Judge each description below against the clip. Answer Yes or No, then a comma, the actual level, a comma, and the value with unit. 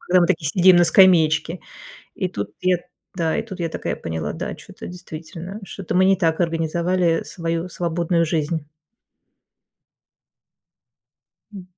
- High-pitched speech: No, medium, 170 Hz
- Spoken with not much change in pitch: Yes, narrow, 2.0 semitones